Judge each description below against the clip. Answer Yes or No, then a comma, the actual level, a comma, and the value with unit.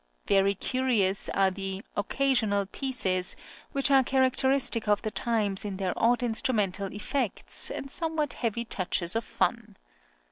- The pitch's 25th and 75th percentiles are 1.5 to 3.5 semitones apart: No, average, 4.9 semitones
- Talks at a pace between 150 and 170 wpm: No, slow, 135 wpm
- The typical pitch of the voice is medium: No, high, 220 Hz